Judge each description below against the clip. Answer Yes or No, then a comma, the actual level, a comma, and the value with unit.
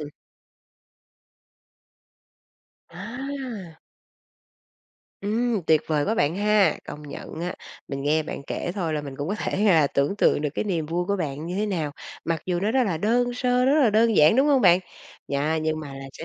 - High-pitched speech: No, medium, 180 Hz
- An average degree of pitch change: No, wide, 6.0 semitones